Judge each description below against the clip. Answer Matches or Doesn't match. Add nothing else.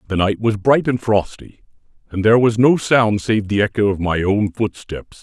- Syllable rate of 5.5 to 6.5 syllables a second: Doesn't match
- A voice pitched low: Matches